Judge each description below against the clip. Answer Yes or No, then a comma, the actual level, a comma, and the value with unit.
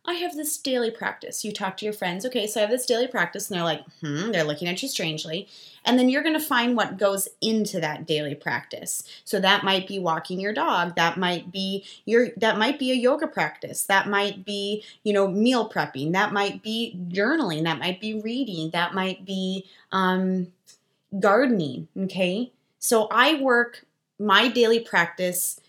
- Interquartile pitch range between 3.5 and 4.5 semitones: Yes, average, 4.2 semitones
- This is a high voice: Yes, high, 200 Hz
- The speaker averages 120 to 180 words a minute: No, average, 190 wpm